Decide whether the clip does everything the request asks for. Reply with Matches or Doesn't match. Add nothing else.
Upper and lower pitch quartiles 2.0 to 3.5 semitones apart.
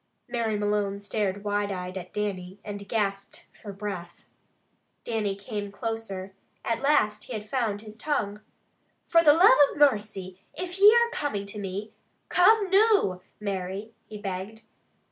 Matches